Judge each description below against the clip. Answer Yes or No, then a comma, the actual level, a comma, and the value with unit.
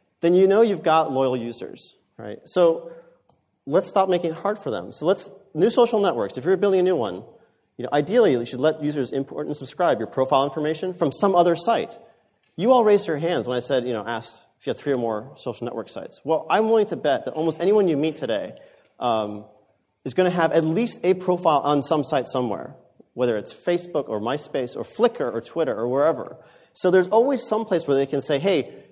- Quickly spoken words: Yes, fast, 225 wpm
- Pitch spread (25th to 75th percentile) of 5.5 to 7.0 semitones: Yes, wide, 6.5 semitones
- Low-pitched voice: No, medium, 165 Hz